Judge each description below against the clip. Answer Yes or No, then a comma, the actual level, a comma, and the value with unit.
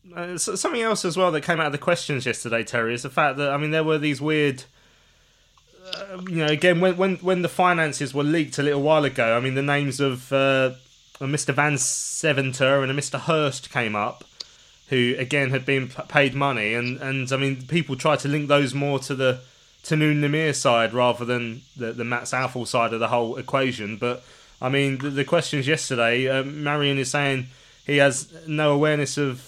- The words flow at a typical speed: No, fast, 210 wpm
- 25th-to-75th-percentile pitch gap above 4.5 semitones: No, average, 2.9 semitones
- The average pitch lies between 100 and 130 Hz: No, medium, 140 Hz